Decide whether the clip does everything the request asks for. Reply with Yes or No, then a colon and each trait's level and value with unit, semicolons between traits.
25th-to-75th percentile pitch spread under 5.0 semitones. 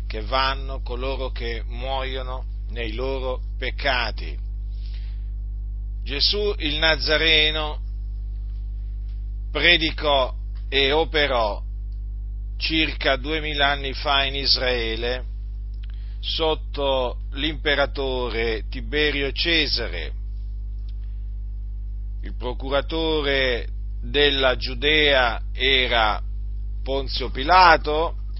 No: wide, 5.6 semitones